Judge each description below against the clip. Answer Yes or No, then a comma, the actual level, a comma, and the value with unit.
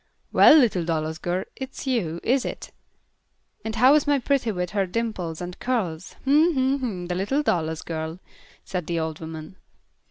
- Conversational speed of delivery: Yes, average, 170 wpm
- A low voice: No, high, 190 Hz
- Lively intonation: Yes, wide, 7.7 semitones